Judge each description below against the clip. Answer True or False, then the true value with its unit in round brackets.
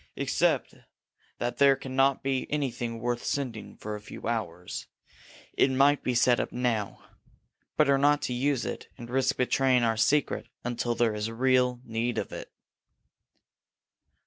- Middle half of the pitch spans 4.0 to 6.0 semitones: False (2.6 semitones)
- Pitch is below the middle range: True (125 Hz)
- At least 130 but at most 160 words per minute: True (150 wpm)